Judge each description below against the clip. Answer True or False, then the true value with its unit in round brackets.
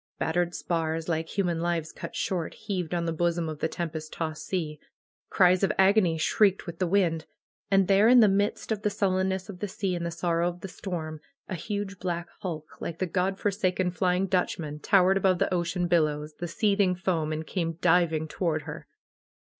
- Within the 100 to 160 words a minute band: False (195 wpm)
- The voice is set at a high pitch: False (175 Hz)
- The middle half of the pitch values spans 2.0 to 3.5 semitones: True (2.7 semitones)